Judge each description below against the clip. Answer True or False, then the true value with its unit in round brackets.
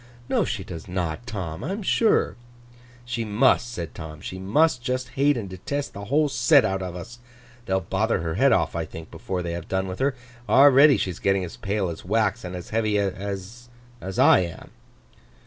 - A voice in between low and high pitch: False (100 Hz)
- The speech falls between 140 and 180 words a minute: False (190 wpm)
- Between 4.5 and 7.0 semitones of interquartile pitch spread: True (5.1 semitones)